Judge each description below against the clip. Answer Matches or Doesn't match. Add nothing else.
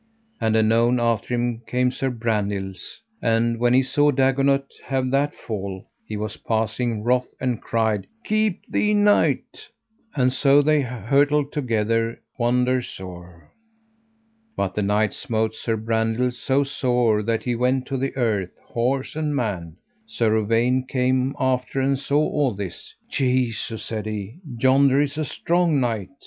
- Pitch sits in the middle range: Doesn't match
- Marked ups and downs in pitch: Doesn't match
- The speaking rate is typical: Matches